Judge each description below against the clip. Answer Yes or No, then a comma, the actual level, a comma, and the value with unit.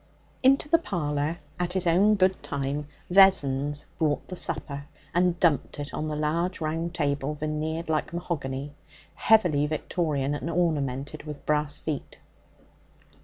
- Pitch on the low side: No, medium, 155 Hz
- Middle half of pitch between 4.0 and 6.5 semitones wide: No, average, 3.3 semitones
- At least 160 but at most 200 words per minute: No, slow, 135 wpm